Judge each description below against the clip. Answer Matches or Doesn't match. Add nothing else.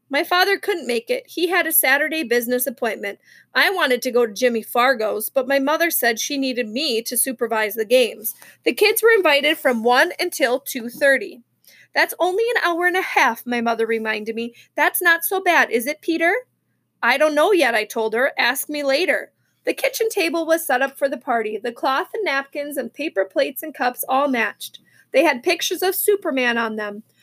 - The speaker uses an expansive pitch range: Matches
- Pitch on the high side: Matches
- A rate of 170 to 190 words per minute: Doesn't match